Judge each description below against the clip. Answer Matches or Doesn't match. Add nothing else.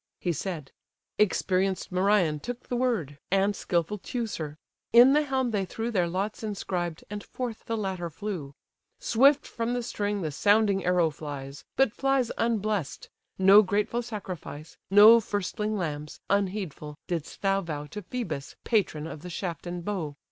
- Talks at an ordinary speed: Matches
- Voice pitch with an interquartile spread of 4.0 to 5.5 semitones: Matches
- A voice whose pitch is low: Doesn't match